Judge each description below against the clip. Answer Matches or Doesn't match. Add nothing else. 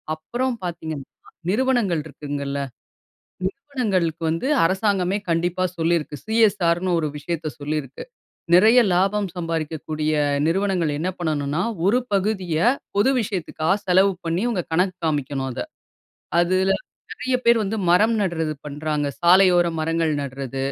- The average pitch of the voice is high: Doesn't match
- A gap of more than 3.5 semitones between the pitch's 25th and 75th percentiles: Matches